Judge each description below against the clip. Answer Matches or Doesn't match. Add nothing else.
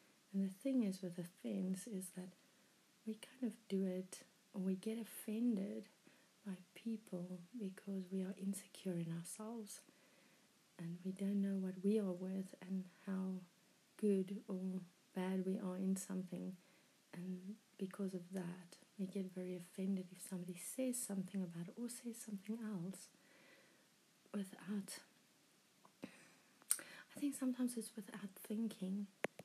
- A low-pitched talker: Doesn't match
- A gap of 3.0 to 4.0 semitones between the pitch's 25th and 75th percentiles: Doesn't match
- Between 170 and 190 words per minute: Doesn't match